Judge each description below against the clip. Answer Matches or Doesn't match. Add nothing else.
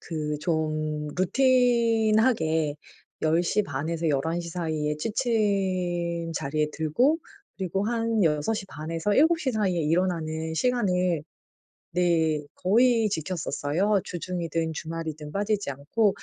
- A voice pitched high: Doesn't match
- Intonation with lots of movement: Doesn't match